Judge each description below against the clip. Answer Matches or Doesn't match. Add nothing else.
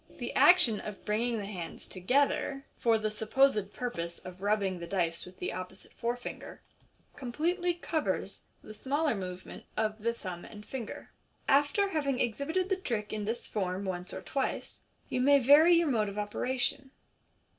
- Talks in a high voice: Matches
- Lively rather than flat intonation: Matches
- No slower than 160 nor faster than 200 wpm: Matches